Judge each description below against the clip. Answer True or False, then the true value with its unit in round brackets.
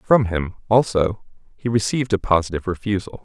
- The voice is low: True (100 Hz)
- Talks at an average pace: True (150 wpm)